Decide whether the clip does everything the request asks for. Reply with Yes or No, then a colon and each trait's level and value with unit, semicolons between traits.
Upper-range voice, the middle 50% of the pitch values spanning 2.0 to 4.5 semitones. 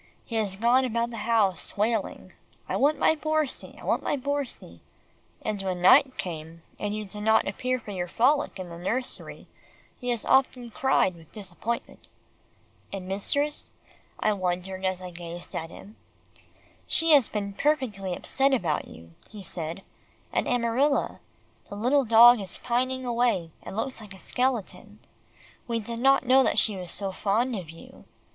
No: high, 220 Hz; average, 5.2 semitones